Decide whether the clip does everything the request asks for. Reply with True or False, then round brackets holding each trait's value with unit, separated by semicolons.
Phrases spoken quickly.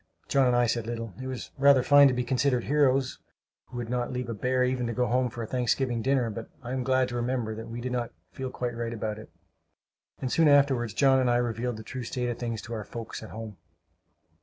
True (245 wpm)